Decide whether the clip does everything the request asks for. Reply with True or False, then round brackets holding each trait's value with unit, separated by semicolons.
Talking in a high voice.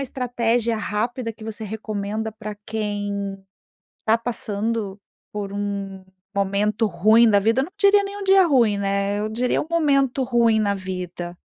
True (215 Hz)